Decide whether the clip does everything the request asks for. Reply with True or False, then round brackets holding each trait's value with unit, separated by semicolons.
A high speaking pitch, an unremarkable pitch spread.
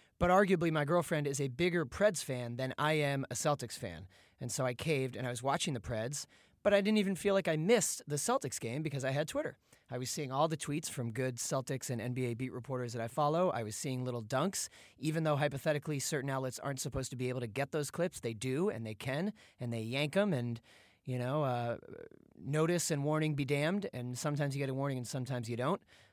False (140 Hz; 3.9 semitones)